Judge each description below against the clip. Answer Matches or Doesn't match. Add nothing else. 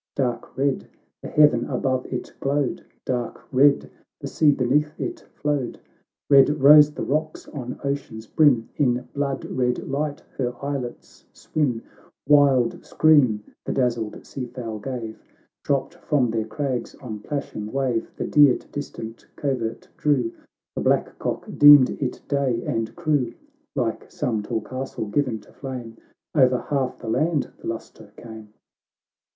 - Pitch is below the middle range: Matches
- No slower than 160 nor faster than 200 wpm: Doesn't match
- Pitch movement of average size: Matches